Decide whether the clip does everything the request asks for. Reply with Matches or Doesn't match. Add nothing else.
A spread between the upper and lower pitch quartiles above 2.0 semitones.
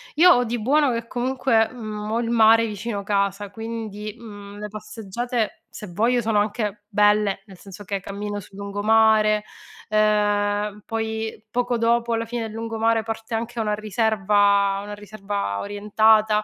Doesn't match